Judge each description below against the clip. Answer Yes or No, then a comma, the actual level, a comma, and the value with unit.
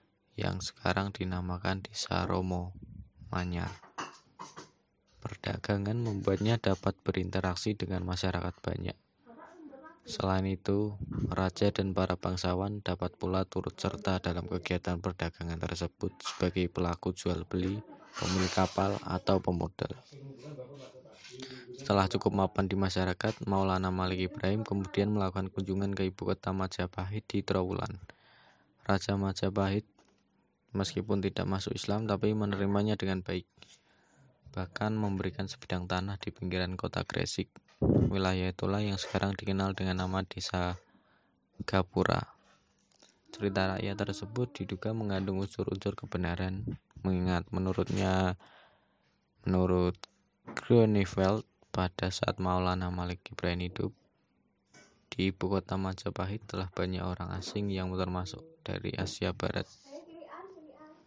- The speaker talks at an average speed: Yes, average, 110 wpm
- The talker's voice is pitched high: No, very low, 95 Hz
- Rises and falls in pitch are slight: Yes, narrow, 1.9 semitones